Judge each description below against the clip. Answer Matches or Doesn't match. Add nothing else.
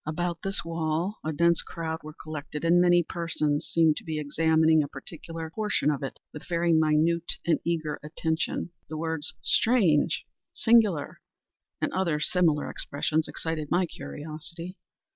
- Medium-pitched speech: Matches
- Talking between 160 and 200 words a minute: Doesn't match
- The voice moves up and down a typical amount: Doesn't match